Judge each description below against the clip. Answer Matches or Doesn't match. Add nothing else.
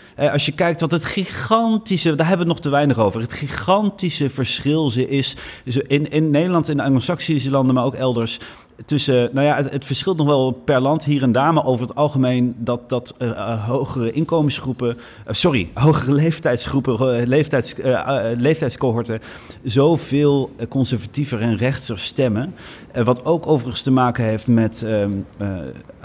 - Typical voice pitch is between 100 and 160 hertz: Matches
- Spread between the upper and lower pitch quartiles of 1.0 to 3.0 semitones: Doesn't match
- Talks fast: Doesn't match